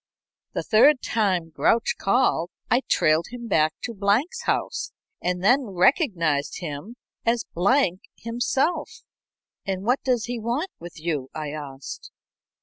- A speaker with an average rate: No, slow, 130 wpm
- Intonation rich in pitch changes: Yes, wide, 6.8 semitones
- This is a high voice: Yes, high, 200 Hz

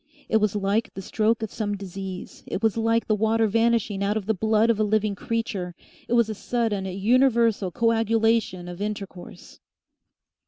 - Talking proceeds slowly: No, average, 170 wpm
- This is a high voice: Yes, high, 215 Hz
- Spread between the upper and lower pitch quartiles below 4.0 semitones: Yes, narrow, 2.4 semitones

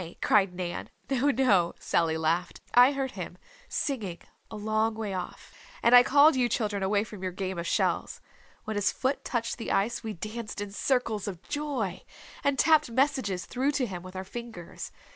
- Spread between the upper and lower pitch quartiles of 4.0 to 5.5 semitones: Yes, average, 5.2 semitones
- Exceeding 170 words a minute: Yes, average, 180 wpm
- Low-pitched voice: No, high, 215 Hz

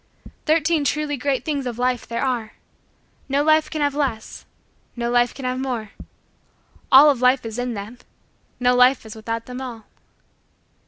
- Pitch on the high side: Yes, very high, 250 Hz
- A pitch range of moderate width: Yes, average, 3.1 semitones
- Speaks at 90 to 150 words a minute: No, average, 165 wpm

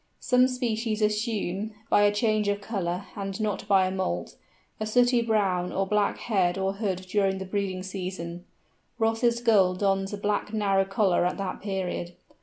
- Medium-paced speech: Yes, average, 170 wpm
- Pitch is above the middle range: Yes, high, 200 Hz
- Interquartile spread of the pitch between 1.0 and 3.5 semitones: Yes, narrow, 2.4 semitones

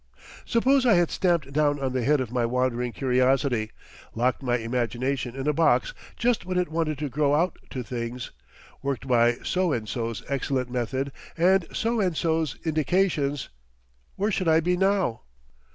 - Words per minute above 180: No, average, 170 wpm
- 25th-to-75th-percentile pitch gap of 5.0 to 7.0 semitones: Yes, wide, 5.6 semitones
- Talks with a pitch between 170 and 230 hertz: No, medium, 140 Hz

